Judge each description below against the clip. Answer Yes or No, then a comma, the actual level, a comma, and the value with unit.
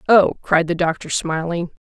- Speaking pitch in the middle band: Yes, medium, 170 Hz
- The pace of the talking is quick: No, average, 165 wpm